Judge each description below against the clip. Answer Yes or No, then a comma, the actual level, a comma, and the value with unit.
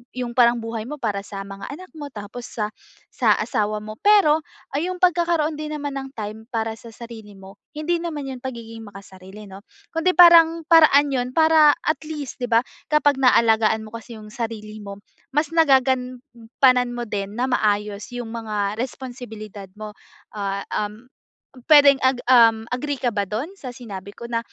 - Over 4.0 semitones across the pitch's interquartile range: Yes, average, 5.1 semitones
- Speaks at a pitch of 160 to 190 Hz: No, high, 240 Hz